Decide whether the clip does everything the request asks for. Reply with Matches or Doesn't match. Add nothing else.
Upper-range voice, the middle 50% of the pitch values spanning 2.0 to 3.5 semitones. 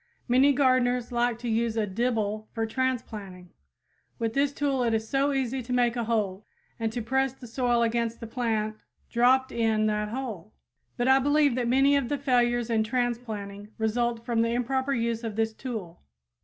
Matches